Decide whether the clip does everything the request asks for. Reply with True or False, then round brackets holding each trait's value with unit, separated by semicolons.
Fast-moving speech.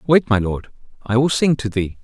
True (235 wpm)